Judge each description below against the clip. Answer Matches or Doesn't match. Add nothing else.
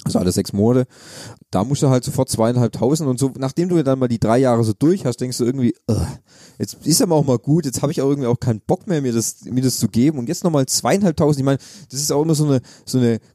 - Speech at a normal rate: Doesn't match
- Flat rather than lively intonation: Doesn't match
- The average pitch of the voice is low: Matches